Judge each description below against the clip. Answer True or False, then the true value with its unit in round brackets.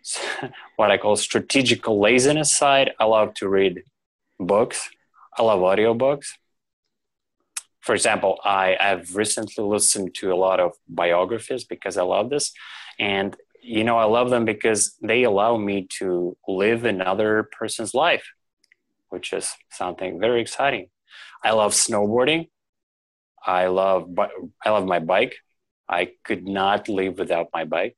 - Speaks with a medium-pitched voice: False (105 Hz)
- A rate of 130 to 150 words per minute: True (135 wpm)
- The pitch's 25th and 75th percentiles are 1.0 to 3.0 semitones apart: False (3.6 semitones)